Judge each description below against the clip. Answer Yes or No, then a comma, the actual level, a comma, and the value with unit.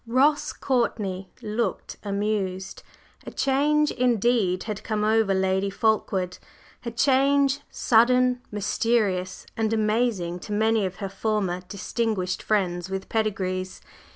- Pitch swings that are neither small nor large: Yes, average, 3.8 semitones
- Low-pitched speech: No, high, 215 Hz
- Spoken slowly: Yes, slow, 115 wpm